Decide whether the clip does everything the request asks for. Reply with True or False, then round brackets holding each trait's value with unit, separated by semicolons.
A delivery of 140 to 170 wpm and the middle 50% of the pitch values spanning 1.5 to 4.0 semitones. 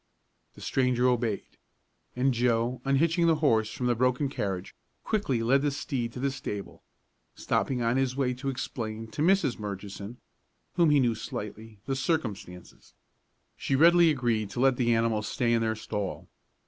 True (160 wpm; 3.6 semitones)